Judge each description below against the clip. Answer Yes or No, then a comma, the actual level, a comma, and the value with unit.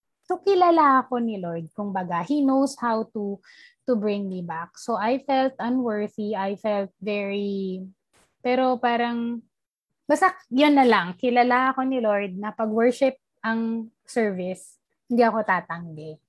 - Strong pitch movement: No, average, 4.4 semitones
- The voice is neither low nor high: No, high, 225 Hz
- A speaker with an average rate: Yes, average, 145 wpm